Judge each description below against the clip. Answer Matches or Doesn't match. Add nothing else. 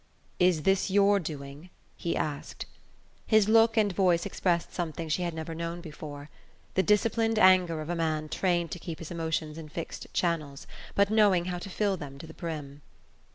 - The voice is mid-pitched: Matches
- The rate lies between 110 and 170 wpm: Doesn't match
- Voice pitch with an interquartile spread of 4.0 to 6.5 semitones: Doesn't match